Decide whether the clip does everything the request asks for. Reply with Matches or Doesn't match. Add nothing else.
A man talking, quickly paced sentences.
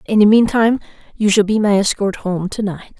Doesn't match